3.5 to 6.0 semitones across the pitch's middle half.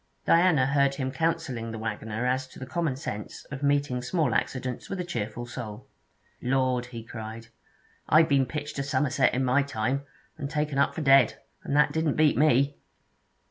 No: average, 3.1 semitones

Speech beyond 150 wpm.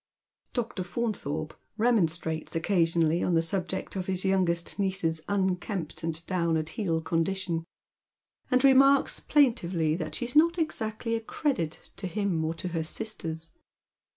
No: average, 140 wpm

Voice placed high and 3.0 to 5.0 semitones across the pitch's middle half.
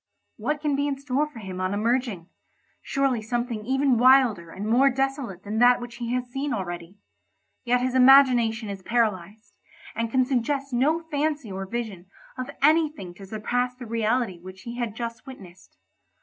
Yes: high, 240 Hz; average, 4.3 semitones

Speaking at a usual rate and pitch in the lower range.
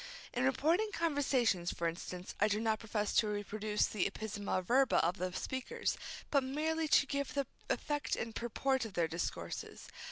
No: average, 165 wpm; high, 225 Hz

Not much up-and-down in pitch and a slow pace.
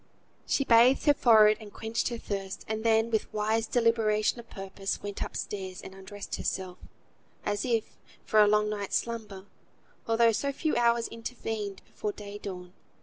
No: narrow, 2.3 semitones; average, 160 wpm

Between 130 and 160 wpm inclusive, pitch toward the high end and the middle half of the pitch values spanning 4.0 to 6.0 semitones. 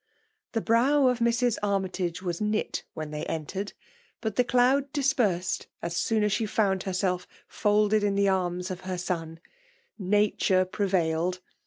No: average, 150 wpm; high, 195 Hz; average, 3.3 semitones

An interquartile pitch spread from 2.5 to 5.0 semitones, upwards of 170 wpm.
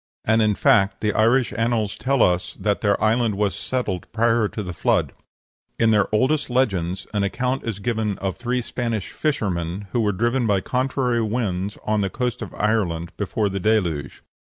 Yes: average, 3.3 semitones; average, 180 wpm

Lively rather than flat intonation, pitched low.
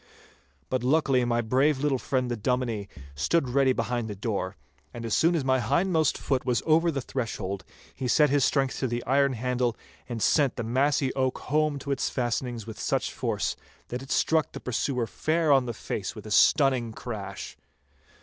No: average, 2.9 semitones; low, 130 Hz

